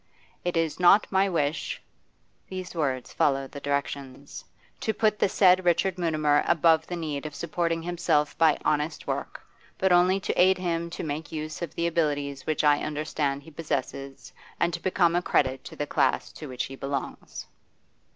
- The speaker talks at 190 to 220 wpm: No, average, 175 wpm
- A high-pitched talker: No, medium, 160 Hz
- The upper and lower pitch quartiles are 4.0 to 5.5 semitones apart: No, average, 3.3 semitones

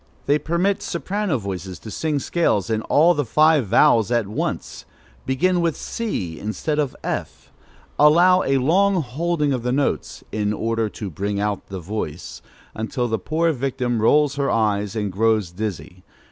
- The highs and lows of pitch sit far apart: Yes, wide, 6.8 semitones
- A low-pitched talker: Yes, low, 120 Hz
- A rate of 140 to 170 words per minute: Yes, average, 160 wpm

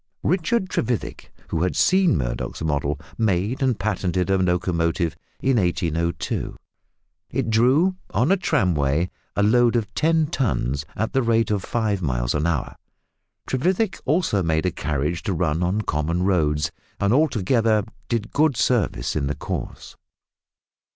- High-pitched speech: No, very low, 95 Hz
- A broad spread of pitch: Yes, wide, 7.1 semitones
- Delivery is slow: No, average, 145 wpm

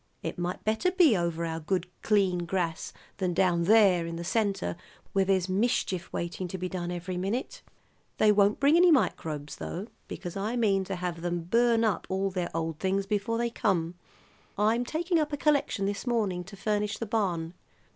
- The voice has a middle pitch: No, high, 195 Hz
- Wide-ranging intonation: No, average, 4.0 semitones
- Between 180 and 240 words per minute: Yes, average, 185 wpm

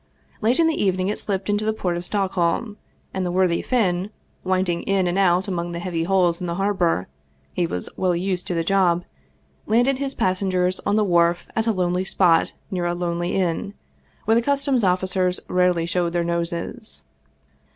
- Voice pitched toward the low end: No, medium, 185 Hz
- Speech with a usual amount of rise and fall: No, narrow, 2.3 semitones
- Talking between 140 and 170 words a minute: No, average, 185 wpm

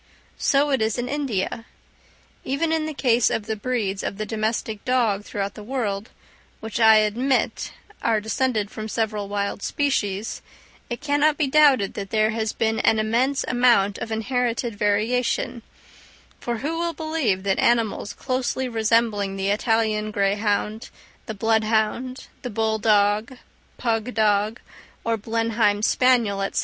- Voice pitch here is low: No, high, 225 Hz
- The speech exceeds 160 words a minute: No, average, 145 wpm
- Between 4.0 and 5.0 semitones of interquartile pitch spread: No, average, 3.1 semitones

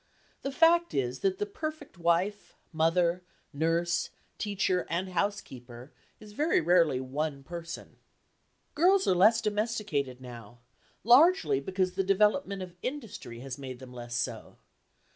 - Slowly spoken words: Yes, slow, 130 wpm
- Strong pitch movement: Yes, wide, 7.4 semitones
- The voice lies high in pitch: No, medium, 180 Hz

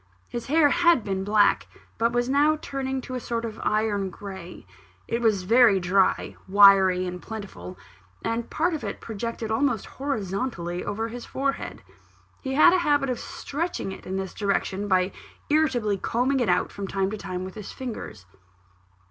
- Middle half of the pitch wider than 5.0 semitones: Yes, wide, 5.4 semitones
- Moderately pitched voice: No, high, 220 Hz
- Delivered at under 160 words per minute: No, average, 170 wpm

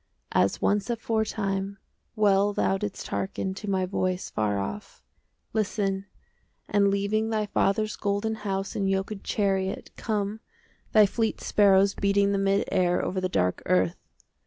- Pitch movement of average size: No, narrow, 1.4 semitones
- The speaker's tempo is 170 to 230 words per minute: No, average, 145 wpm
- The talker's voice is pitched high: Yes, high, 200 Hz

